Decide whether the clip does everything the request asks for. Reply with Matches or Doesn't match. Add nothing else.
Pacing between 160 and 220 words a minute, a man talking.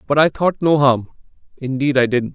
Matches